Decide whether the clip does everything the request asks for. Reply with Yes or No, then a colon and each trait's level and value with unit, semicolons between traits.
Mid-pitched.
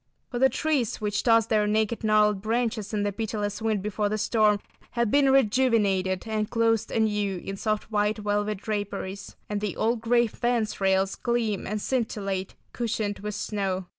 No: high, 215 Hz